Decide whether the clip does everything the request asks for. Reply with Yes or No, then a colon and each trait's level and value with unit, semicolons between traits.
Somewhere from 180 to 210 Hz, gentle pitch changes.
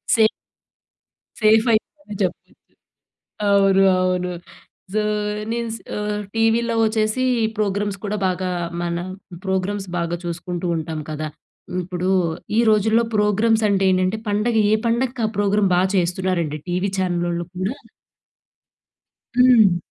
No: high, 200 Hz; average, 3.2 semitones